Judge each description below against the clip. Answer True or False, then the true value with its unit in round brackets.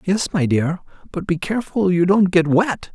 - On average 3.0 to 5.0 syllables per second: True (4.7 syllables/s)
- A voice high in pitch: False (180 Hz)